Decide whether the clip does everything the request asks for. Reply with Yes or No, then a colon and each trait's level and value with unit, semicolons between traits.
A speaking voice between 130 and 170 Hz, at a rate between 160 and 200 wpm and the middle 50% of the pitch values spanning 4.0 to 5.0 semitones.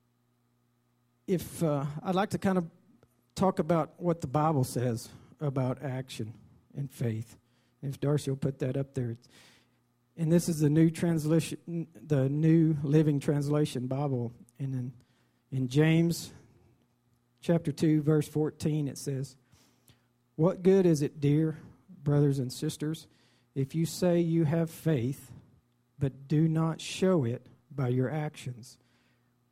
No: medium, 140 Hz; slow, 135 wpm; average, 4.5 semitones